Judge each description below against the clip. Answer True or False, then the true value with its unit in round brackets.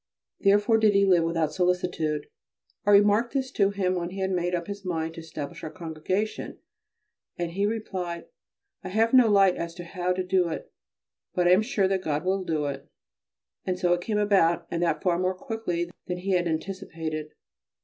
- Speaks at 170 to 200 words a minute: True (190 wpm)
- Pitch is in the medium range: True (180 Hz)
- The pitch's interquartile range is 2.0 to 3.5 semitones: True (2.9 semitones)